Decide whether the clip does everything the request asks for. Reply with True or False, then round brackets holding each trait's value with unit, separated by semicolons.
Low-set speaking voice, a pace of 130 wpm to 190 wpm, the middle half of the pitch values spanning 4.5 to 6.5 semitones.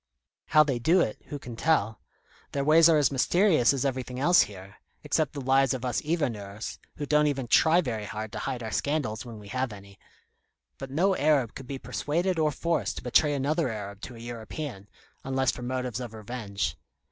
False (130 Hz; 200 wpm; 5.1 semitones)